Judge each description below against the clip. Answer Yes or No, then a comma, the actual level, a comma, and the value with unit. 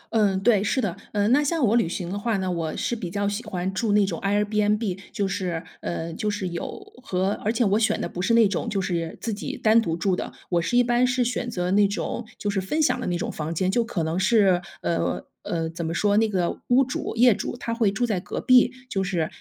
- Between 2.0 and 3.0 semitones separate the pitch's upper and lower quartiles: No, average, 4.3 semitones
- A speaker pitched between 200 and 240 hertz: Yes, high, 205 Hz